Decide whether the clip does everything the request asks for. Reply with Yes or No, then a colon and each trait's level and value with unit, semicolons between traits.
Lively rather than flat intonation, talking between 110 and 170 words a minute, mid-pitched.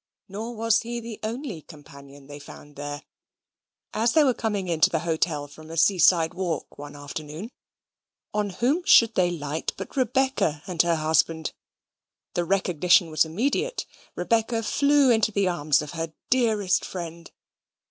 Yes: wide, 6.3 semitones; average, 155 wpm; medium, 180 Hz